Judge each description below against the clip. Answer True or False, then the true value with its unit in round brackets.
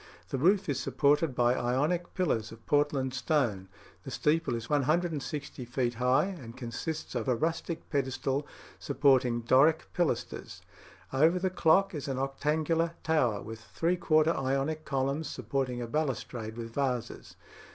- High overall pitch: False (135 Hz)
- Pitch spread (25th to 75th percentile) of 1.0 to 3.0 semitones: False (4.4 semitones)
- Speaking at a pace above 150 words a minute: False (140 wpm)